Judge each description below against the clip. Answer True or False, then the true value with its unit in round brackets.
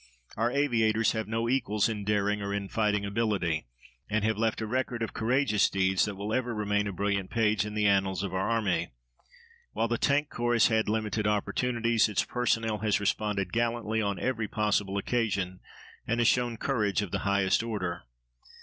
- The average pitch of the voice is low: True (105 Hz)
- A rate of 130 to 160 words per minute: False (185 wpm)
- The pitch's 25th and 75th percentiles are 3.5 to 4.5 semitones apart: False (2.4 semitones)